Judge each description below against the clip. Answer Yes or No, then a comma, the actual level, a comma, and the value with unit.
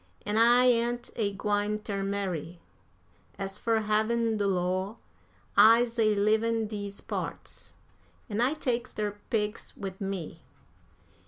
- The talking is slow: Yes, slow, 130 wpm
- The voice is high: Yes, high, 210 Hz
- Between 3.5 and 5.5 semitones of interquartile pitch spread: No, narrow, 2.4 semitones